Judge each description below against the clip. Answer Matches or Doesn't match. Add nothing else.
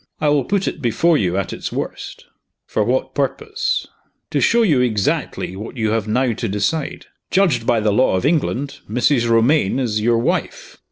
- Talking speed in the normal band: Matches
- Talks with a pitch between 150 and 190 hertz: Doesn't match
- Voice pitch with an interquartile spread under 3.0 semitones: Doesn't match